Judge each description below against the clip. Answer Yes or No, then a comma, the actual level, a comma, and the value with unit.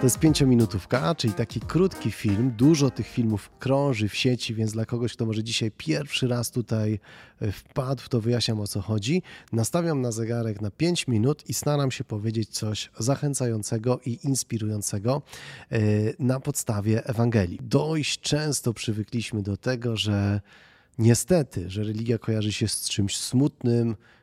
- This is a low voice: Yes, low, 120 Hz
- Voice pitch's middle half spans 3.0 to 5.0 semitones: Yes, average, 3.5 semitones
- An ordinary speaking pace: Yes, average, 145 wpm